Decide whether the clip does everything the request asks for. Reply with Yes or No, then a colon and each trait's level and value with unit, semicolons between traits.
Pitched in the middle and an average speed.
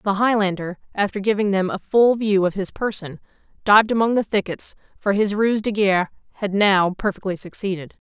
No: high, 200 Hz; average, 180 wpm